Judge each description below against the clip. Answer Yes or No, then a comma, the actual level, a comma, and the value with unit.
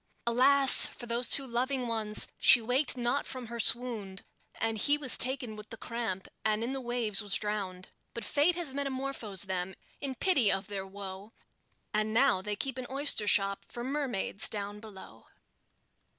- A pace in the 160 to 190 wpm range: Yes, average, 170 wpm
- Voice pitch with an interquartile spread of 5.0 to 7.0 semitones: No, average, 4.1 semitones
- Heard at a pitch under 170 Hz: No, high, 235 Hz